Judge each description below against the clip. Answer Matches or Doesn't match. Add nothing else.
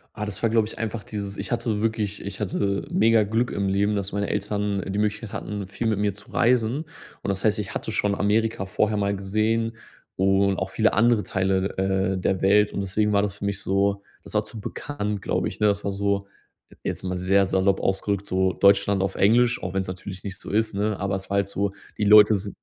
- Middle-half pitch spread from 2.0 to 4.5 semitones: Doesn't match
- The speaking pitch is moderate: Doesn't match